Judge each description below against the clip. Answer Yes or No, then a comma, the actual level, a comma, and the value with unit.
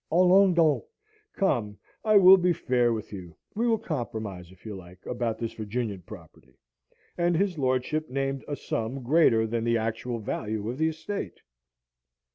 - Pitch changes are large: Yes, wide, 6.8 semitones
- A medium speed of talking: Yes, average, 160 wpm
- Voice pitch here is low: Yes, low, 125 Hz